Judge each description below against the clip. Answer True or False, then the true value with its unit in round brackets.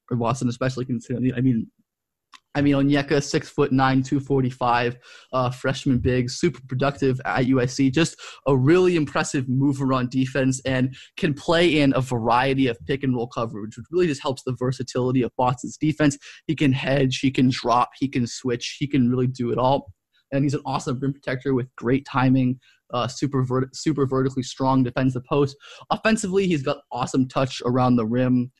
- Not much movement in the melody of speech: True (2.0 semitones)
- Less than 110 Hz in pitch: False (130 Hz)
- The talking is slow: False (185 wpm)